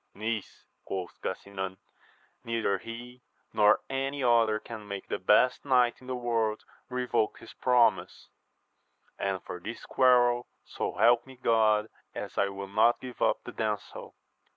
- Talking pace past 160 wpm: No, average, 145 wpm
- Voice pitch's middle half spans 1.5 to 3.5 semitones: Yes, average, 2.9 semitones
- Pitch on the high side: No, low, 115 Hz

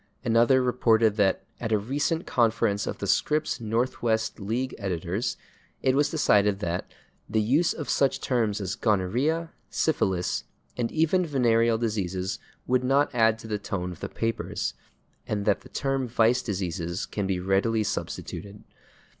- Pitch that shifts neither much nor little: Yes, average, 4.2 semitones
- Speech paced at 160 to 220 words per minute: No, average, 150 wpm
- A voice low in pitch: Yes, low, 115 Hz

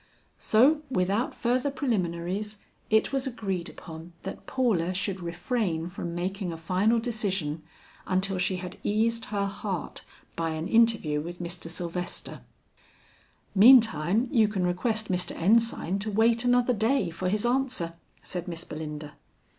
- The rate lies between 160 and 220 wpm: No, average, 140 wpm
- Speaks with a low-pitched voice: No, high, 195 Hz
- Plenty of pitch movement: No, average, 4.8 semitones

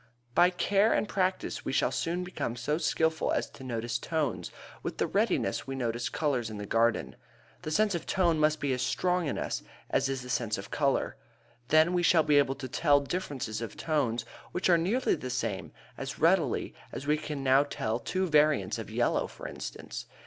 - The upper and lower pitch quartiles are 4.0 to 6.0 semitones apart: Yes, wide, 5.4 semitones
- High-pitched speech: No, medium, 145 Hz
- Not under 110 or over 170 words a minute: No, average, 195 wpm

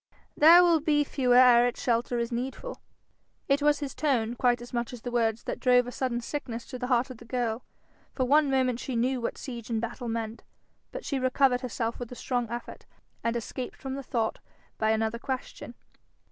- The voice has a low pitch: No, high, 245 Hz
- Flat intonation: Yes, narrow, 2.2 semitones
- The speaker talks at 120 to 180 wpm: No, fast, 205 wpm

